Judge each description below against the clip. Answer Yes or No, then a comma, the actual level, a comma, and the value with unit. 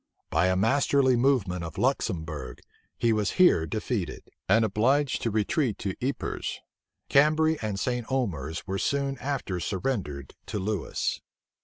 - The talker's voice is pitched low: Yes, low, 110 Hz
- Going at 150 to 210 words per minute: No, slow, 135 wpm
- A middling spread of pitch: No, wide, 6.6 semitones